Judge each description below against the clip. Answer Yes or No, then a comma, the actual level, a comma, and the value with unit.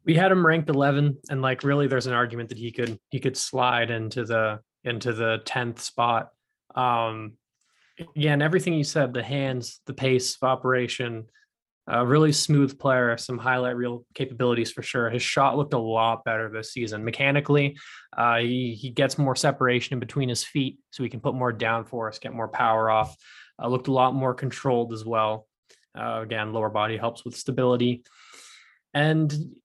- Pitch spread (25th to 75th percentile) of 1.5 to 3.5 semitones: Yes, average, 2.9 semitones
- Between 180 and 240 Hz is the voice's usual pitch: No, low, 125 Hz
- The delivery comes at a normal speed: Yes, average, 185 wpm